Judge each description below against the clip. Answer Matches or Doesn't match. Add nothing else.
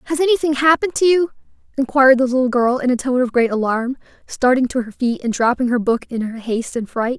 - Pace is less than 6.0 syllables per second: Doesn't match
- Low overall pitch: Doesn't match